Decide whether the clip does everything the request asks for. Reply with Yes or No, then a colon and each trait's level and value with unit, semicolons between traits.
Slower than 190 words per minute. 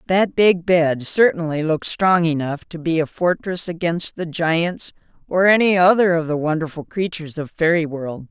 Yes: average, 175 wpm